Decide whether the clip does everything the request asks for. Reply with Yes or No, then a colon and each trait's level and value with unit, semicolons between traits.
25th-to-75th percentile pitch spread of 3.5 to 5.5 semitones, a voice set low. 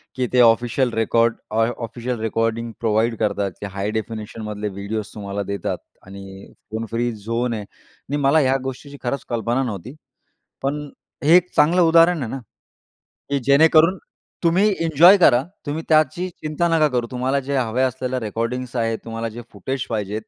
Yes: average, 4.2 semitones; low, 120 Hz